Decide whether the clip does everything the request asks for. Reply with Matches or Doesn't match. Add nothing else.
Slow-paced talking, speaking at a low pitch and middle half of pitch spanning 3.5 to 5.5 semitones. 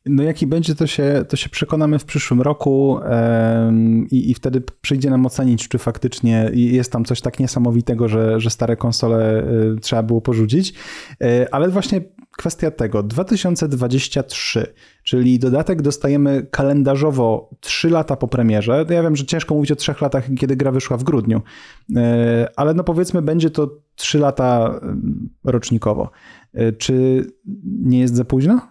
Doesn't match